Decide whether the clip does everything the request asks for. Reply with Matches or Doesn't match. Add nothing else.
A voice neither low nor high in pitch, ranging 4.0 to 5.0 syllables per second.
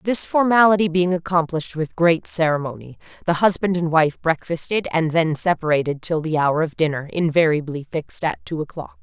Doesn't match